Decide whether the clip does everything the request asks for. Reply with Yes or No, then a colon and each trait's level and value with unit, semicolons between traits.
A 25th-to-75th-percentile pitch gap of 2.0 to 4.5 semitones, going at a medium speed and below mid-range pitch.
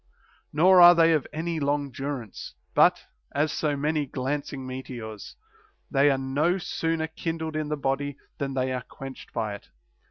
No: average, 3.1 semitones; average, 160 wpm; medium, 145 Hz